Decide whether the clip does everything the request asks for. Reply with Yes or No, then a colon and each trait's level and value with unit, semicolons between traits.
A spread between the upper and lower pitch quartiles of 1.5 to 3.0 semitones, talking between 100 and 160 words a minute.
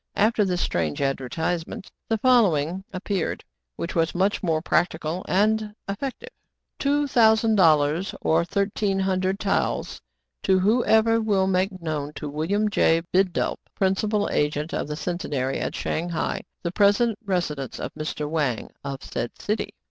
No: average, 4.8 semitones; average, 155 wpm